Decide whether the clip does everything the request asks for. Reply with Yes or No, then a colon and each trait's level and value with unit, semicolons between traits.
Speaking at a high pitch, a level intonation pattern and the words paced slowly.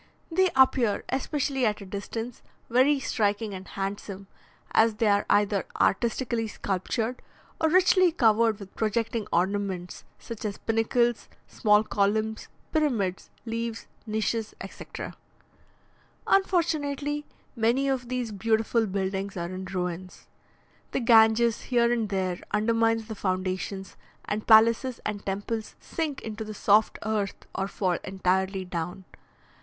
No: high, 220 Hz; average, 3.2 semitones; slow, 125 wpm